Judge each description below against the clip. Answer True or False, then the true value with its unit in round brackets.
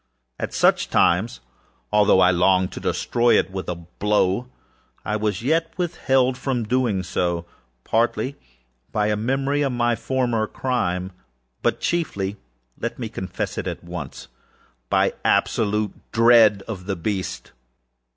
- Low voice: True (105 Hz)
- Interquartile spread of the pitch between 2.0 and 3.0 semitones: False (4.9 semitones)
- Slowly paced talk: True (130 wpm)